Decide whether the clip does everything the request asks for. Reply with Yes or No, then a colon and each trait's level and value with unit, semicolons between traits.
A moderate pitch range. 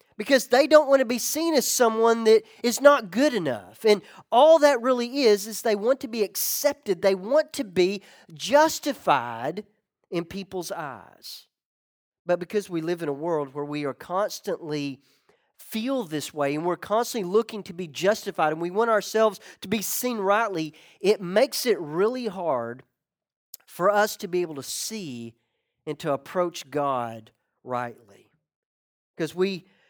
No: wide, 6.8 semitones